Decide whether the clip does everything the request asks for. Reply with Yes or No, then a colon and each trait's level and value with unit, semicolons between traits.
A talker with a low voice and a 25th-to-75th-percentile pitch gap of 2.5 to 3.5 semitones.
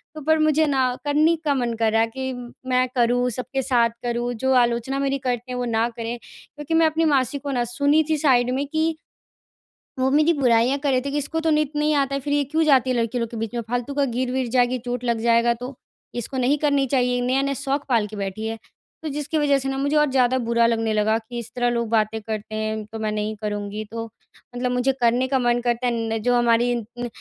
No: very high, 250 Hz; average, 3.1 semitones